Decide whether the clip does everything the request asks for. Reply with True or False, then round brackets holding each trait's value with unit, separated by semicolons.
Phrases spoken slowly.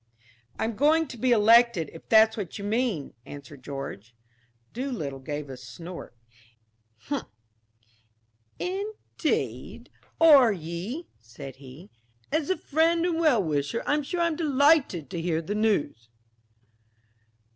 True (120 wpm)